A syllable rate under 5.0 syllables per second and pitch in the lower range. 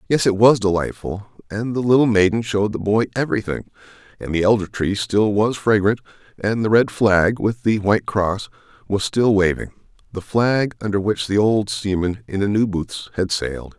No: 5.1 syllables/s; low, 105 Hz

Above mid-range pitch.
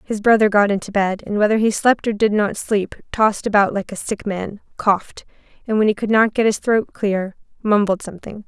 Yes: high, 210 Hz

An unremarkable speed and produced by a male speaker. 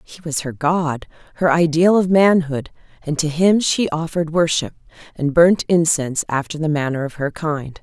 No: average, 175 wpm; female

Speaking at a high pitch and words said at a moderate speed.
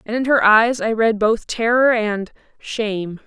Yes: high, 225 Hz; average, 165 wpm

